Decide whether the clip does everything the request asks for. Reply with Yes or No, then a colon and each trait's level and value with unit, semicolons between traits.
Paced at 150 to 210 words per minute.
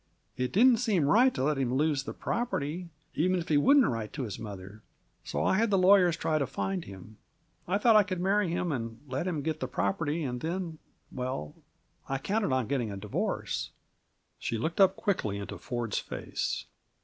Yes: average, 195 wpm